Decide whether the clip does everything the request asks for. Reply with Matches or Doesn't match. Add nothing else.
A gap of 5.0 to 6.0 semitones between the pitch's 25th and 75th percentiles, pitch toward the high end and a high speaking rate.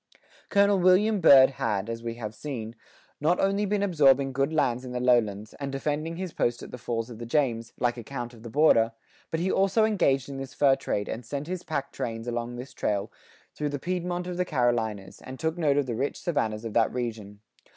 Doesn't match